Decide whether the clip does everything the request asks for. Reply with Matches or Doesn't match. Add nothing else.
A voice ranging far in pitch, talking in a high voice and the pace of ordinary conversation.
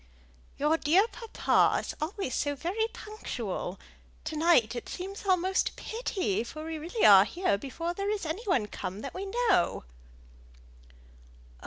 Matches